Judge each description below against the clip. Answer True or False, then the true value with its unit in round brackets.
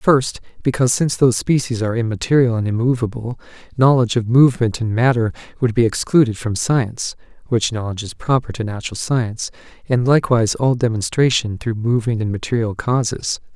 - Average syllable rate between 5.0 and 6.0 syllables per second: True (5.2 syllables/s)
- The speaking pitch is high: False (120 Hz)